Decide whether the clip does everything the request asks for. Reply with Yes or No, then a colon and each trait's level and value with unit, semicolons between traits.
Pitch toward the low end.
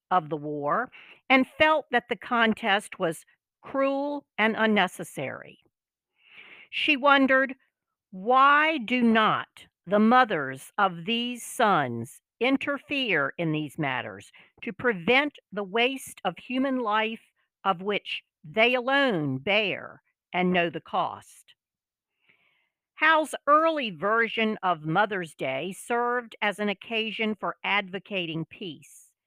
No: high, 220 Hz